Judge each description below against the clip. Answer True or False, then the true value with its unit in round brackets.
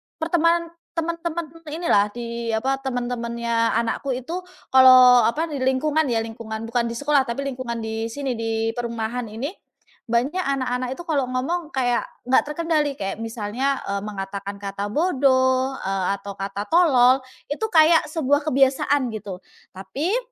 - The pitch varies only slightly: False (4.3 semitones)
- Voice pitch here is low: False (255 Hz)